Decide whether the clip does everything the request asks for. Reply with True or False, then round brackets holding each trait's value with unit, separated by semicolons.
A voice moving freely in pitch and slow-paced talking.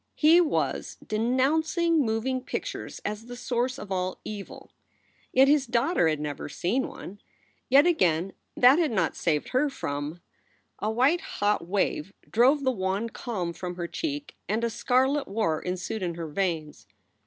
False (6.6 semitones; 155 wpm)